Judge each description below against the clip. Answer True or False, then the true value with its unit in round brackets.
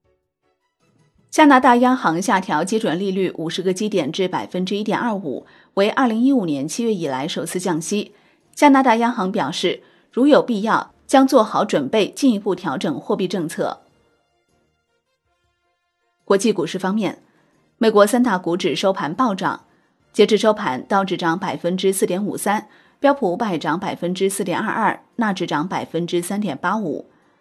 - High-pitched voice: True (195 Hz)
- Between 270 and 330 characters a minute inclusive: False (250 characters per minute)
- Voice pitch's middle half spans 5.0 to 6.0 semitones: False (4.4 semitones)